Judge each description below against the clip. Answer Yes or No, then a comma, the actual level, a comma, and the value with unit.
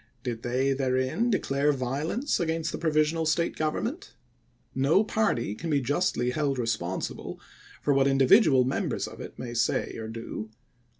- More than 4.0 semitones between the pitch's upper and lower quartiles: Yes, average, 4.4 semitones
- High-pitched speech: No, low, 135 Hz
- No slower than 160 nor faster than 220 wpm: No, average, 145 wpm